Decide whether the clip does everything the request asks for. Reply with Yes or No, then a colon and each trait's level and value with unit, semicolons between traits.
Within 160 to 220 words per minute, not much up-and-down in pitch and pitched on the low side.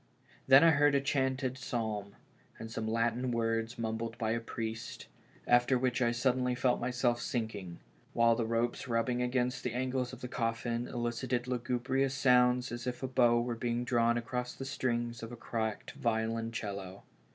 Yes: average, 170 wpm; narrow, 1.7 semitones; low, 120 Hz